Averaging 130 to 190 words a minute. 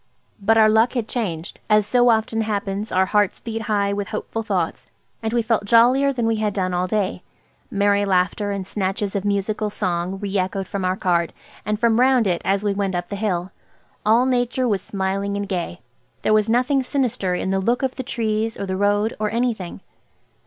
No: average, 200 wpm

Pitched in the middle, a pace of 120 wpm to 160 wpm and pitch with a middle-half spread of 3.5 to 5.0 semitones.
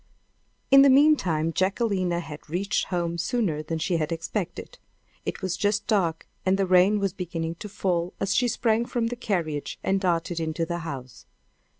No: medium, 180 Hz; average, 175 wpm; average, 3.9 semitones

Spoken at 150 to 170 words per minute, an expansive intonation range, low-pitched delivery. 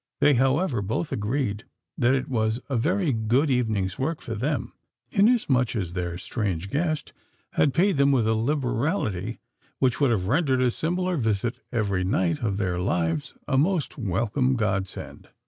Yes: average, 165 wpm; wide, 5.7 semitones; low, 120 Hz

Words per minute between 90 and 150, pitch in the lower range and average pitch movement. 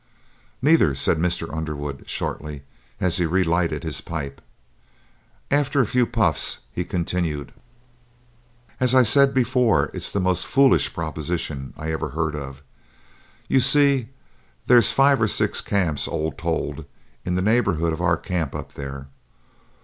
No: average, 140 wpm; very low, 85 Hz; wide, 7.6 semitones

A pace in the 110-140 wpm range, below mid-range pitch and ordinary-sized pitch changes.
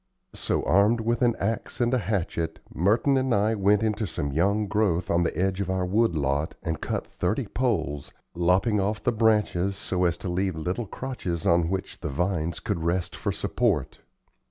No: average, 185 wpm; very low, 95 Hz; average, 4.1 semitones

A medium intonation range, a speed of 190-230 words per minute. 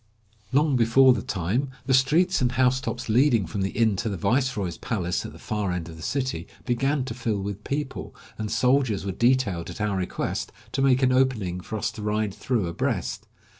Yes: average, 4.6 semitones; average, 200 wpm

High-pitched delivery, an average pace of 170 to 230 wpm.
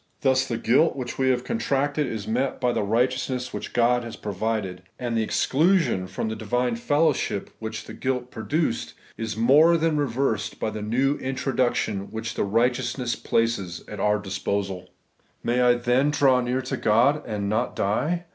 No: low, 120 Hz; average, 180 wpm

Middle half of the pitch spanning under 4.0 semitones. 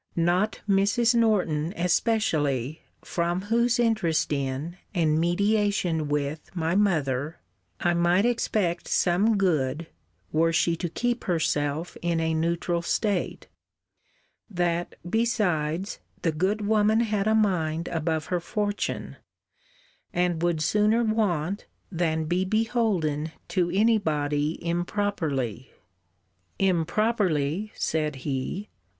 No: average, 4.6 semitones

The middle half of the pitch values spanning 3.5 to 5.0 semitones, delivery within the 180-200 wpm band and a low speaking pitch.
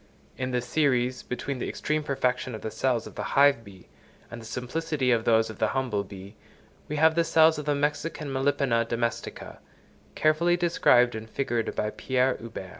Yes: average, 4.2 semitones; average, 185 wpm; low, 130 Hz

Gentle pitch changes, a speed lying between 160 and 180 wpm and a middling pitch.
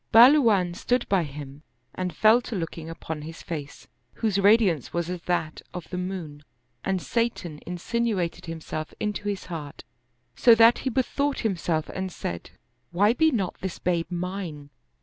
No: average, 5.0 semitones; average, 165 wpm; medium, 180 Hz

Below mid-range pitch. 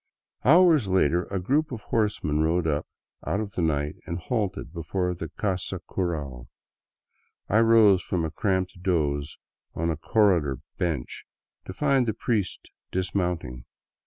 Yes: very low, 90 Hz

